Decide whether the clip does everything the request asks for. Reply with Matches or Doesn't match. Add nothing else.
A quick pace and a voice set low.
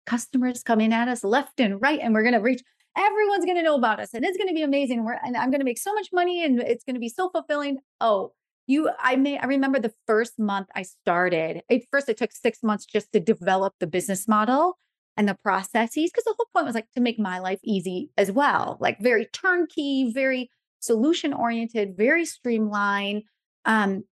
Doesn't match